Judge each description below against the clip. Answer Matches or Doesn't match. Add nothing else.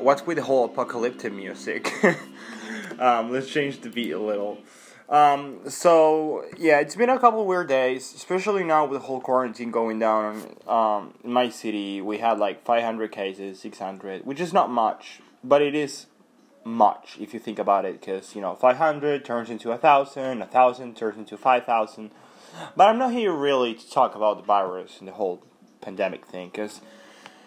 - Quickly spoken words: Doesn't match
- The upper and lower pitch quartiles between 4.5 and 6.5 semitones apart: Matches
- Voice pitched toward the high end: Doesn't match